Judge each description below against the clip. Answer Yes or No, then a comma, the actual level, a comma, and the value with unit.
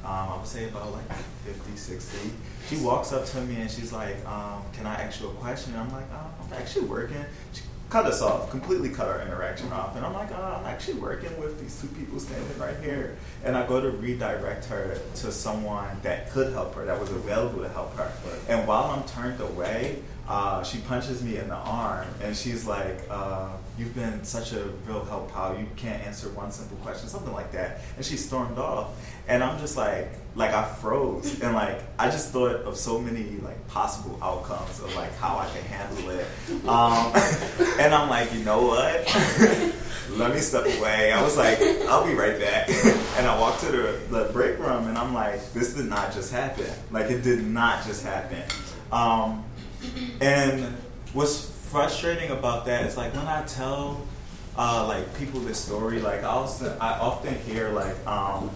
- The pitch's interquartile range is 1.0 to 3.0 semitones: No, average, 3.7 semitones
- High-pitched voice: No, low, 115 Hz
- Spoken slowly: No, average, 200 wpm